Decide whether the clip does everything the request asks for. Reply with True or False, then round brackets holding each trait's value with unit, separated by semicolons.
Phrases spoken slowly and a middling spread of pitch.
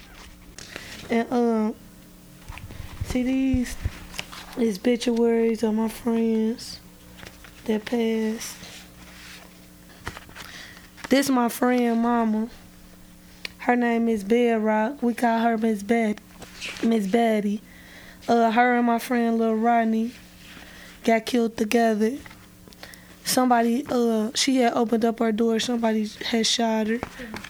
False (110 wpm; 1.4 semitones)